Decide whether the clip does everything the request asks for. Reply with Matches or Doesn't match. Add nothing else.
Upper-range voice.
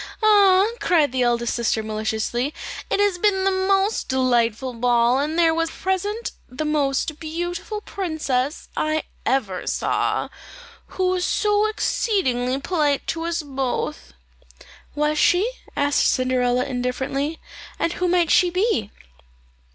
Matches